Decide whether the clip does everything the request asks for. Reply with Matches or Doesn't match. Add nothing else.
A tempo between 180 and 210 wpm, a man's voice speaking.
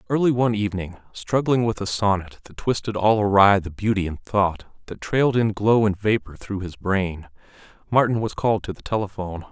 Matches